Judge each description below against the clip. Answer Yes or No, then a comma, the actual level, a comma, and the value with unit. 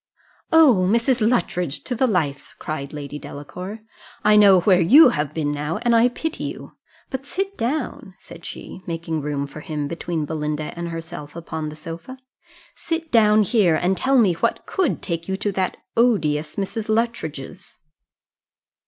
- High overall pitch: No, medium, 180 Hz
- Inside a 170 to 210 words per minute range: No, average, 160 wpm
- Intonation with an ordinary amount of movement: No, wide, 6.8 semitones